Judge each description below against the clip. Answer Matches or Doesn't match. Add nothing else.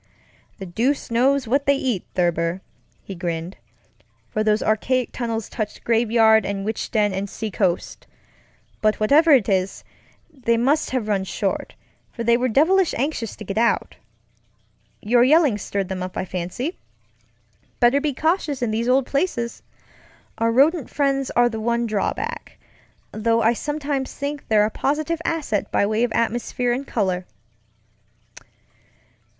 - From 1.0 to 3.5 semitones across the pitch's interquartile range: Doesn't match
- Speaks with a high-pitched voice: Matches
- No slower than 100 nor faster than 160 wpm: Matches